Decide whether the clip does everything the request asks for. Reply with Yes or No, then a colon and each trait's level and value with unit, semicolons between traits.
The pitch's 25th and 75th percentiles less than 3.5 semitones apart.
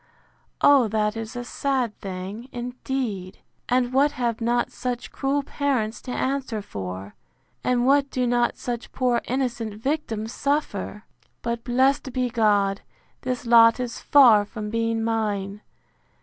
Yes: average, 3.0 semitones